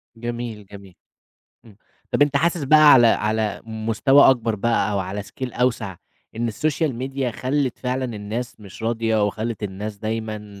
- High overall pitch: No, low, 115 Hz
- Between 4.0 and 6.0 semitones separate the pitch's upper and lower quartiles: No, average, 3.2 semitones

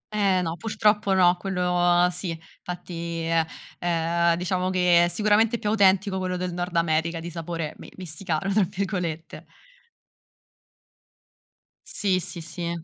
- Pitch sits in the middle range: Yes, medium, 180 Hz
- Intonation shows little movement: Yes, narrow, 2.2 semitones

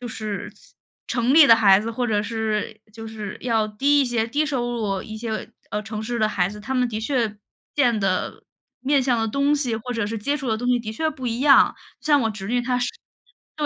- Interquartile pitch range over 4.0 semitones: No, average, 2.9 semitones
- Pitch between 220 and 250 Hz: Yes, high, 230 Hz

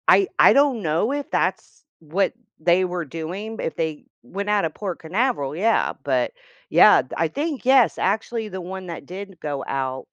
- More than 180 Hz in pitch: Yes, high, 190 Hz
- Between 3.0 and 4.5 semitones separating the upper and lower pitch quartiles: No, wide, 5.5 semitones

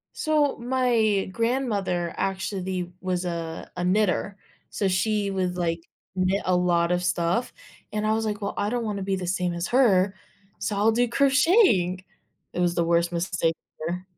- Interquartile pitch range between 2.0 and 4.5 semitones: Yes, average, 3.6 semitones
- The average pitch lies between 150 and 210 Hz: Yes, high, 190 Hz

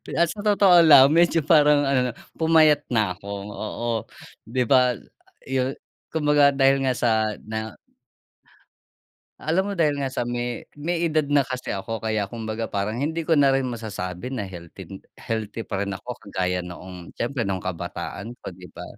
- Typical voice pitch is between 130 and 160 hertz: No, low, 120 Hz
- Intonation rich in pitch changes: Yes, wide, 6.4 semitones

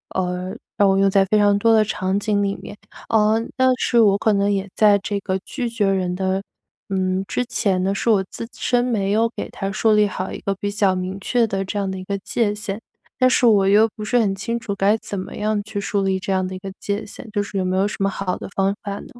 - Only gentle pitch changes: Yes, narrow, 1.8 semitones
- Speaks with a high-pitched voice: Yes, high, 200 Hz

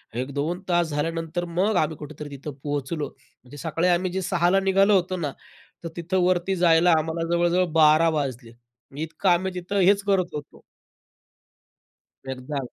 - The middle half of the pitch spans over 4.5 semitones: No, average, 3.5 semitones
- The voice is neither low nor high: Yes, medium, 165 Hz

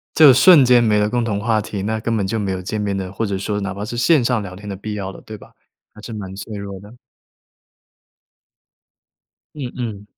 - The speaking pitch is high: No, low, 105 Hz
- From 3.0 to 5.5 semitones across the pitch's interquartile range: No, narrow, 2.6 semitones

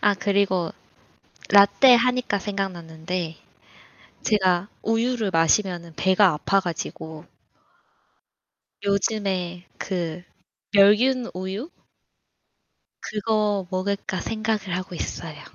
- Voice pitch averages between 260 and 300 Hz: No, high, 195 Hz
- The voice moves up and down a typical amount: Yes, average, 3.0 semitones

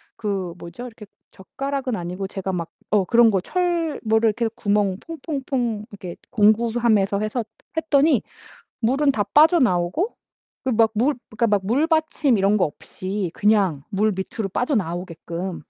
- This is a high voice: Yes, high, 215 Hz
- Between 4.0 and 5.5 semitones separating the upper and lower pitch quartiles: Yes, average, 5.2 semitones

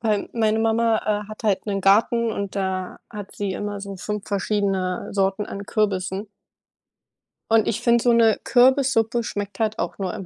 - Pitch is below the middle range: No, high, 210 Hz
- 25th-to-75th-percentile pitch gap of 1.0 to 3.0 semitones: Yes, narrow, 2.4 semitones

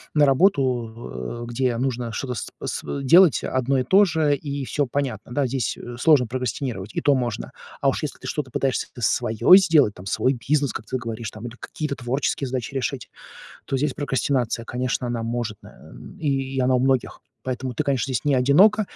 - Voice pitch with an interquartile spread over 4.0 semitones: No, average, 2.9 semitones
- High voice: No, low, 130 Hz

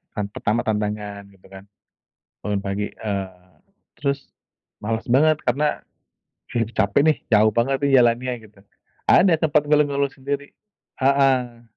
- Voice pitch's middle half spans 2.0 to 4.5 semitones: No, average, 5.1 semitones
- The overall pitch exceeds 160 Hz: No, low, 120 Hz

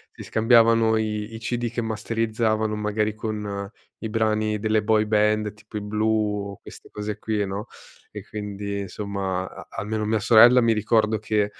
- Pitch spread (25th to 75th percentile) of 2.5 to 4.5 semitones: No, narrow, 1.1 semitones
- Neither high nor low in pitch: No, low, 110 Hz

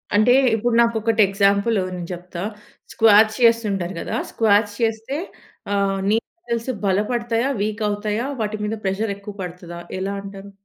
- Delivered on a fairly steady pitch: Yes, narrow, 2.3 semitones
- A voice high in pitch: Yes, high, 210 Hz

